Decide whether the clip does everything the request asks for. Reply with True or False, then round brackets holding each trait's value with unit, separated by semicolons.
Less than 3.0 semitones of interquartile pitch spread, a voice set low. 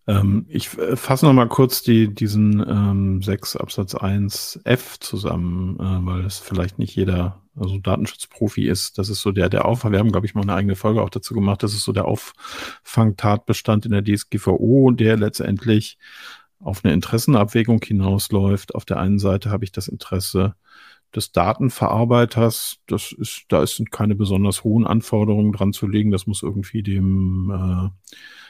True (2.4 semitones; 105 Hz)